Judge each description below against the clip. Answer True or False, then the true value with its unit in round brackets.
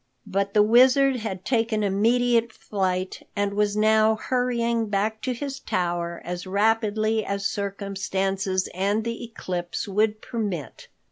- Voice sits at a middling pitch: False (210 Hz)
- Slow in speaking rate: True (130 wpm)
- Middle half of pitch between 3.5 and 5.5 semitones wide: False (2.8 semitones)